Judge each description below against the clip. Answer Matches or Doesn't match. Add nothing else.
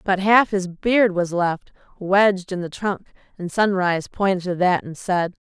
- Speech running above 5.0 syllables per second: Doesn't match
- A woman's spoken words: Matches